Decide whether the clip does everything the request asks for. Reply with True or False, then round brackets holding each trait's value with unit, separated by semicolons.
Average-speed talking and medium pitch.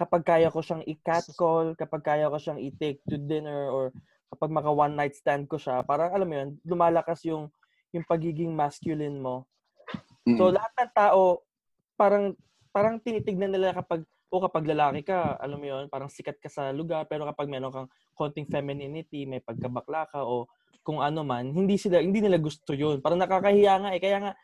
True (185 wpm; 155 Hz)